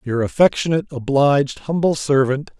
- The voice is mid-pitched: Yes, medium, 145 Hz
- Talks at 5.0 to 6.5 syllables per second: Yes, 5.5 syllables/s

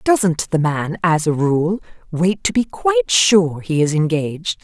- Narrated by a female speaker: Yes, female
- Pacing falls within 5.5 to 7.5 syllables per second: No, 4.0 syllables/s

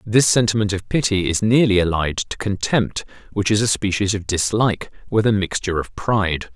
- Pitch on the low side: Yes, low, 100 Hz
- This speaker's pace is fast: No, average, 185 wpm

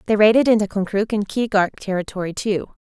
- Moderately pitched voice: No, high, 205 Hz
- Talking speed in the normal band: Yes, average, 170 wpm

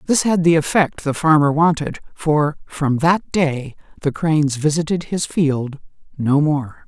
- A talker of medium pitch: Yes, medium, 155 Hz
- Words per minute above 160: No, average, 155 wpm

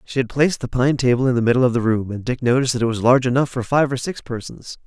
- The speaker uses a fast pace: Yes, fast, 310 wpm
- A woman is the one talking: No, male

